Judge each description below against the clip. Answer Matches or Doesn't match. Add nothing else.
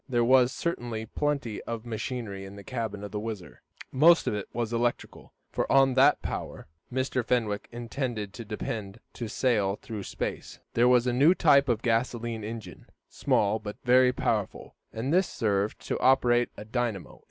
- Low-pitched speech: Matches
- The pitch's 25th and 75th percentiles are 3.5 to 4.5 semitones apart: Doesn't match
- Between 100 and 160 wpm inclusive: Doesn't match